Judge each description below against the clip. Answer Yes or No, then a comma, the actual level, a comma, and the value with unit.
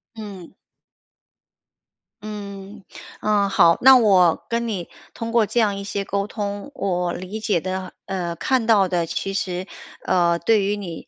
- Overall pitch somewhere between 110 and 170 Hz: No, high, 200 Hz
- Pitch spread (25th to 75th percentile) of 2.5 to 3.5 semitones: Yes, average, 2.8 semitones